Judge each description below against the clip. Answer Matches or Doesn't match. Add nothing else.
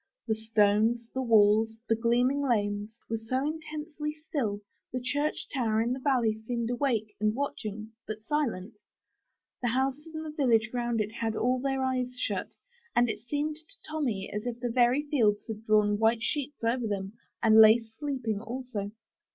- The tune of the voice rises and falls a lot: Doesn't match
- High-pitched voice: Matches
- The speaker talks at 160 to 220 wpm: Matches